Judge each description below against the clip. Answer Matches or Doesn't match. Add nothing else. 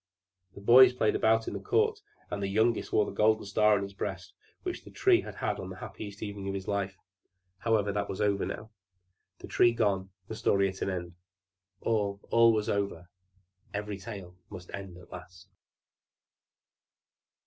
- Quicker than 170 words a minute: Matches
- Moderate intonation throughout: Doesn't match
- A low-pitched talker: Matches